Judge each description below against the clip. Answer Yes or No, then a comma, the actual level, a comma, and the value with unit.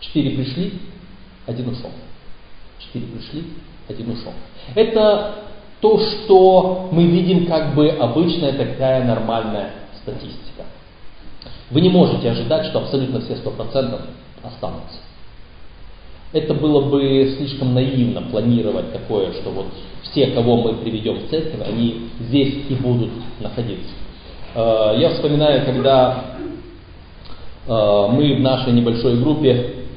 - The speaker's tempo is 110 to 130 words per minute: Yes, average, 115 wpm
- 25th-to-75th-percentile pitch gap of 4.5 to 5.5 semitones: Yes, average, 5.0 semitones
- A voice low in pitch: Yes, low, 130 Hz